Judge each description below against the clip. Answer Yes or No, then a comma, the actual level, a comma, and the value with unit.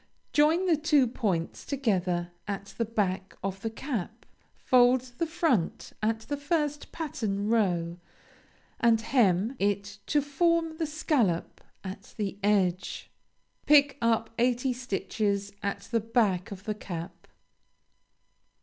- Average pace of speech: No, slow, 125 wpm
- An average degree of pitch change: No, wide, 6.1 semitones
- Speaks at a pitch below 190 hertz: No, high, 225 Hz